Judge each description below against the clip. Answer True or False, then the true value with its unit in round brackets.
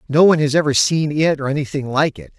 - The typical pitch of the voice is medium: True (145 Hz)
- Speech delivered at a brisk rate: True (250 wpm)